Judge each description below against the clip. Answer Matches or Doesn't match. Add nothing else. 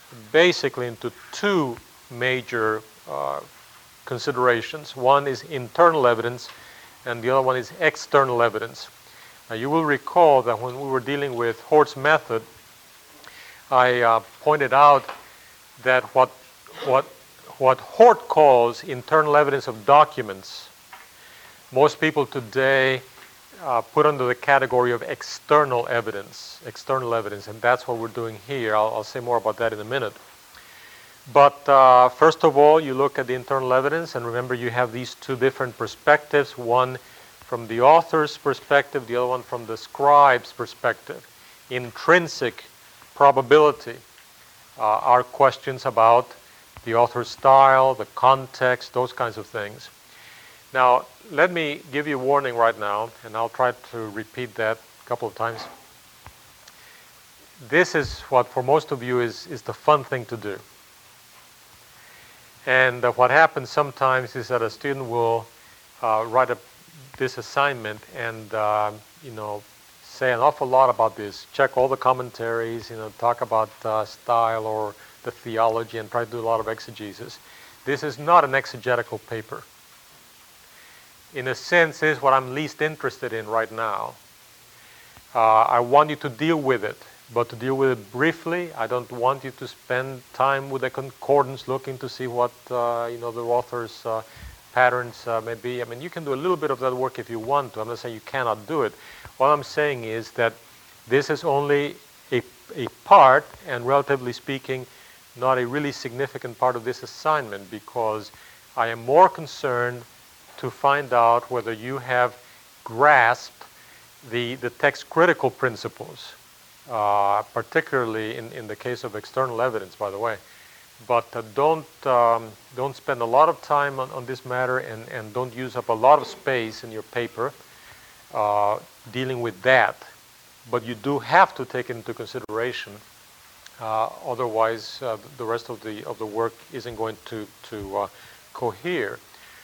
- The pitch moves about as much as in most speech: Matches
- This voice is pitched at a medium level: Doesn't match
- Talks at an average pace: Matches